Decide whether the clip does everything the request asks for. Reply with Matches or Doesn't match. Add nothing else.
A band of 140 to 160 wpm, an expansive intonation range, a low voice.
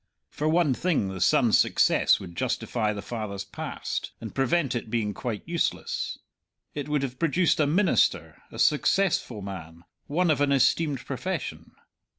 Matches